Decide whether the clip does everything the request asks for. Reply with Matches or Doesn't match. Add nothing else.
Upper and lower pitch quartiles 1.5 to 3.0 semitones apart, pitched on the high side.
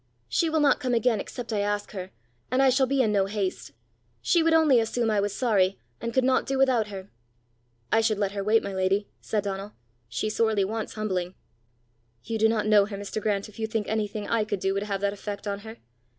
Matches